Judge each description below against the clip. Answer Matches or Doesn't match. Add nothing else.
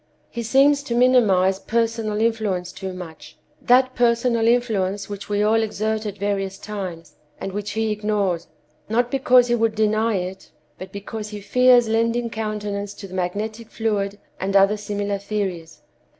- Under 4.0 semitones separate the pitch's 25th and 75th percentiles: Matches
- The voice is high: Matches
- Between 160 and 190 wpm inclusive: Doesn't match